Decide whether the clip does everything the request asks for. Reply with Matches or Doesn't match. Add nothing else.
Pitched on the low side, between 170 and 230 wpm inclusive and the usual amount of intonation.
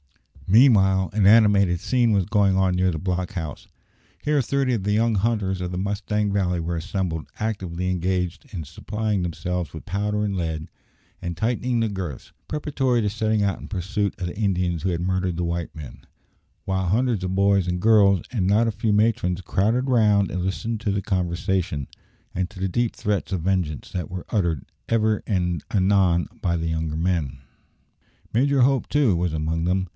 Matches